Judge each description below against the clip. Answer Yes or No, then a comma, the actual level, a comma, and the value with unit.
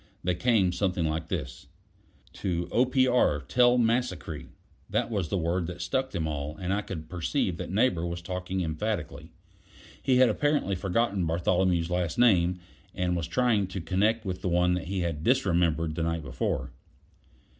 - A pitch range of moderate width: Yes, average, 4.2 semitones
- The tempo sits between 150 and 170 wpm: Yes, average, 160 wpm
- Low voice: Yes, very low, 90 Hz